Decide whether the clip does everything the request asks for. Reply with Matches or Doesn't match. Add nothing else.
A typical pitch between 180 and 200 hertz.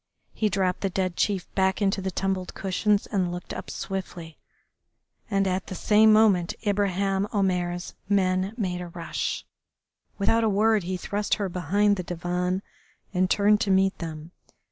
Matches